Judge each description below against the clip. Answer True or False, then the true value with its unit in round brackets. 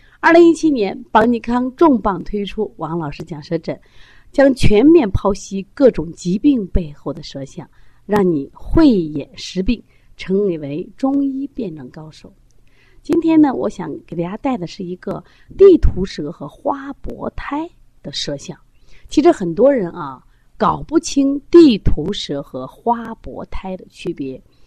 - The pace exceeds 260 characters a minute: False (215 characters per minute)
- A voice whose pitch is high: True (200 Hz)